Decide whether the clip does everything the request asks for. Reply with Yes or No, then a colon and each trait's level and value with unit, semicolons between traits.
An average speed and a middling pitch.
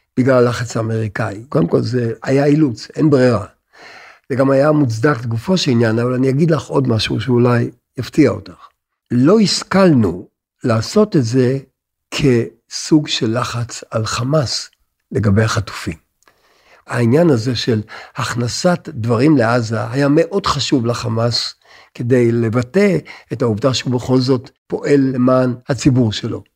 No: average, 135 wpm; low, 125 Hz